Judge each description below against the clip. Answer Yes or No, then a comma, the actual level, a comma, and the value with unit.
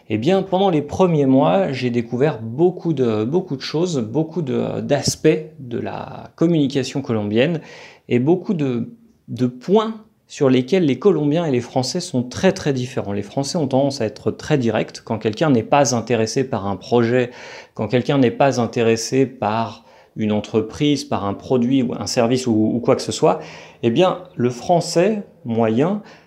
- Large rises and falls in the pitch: Yes, wide, 5.9 semitones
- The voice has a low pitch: Yes, low, 130 Hz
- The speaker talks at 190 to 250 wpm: No, average, 175 wpm